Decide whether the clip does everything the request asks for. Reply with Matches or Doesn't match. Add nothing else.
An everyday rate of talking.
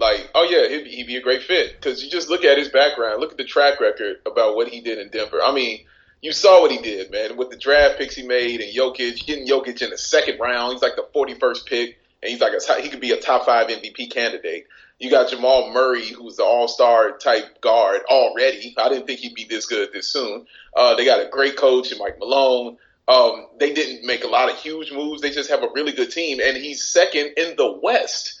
Doesn't match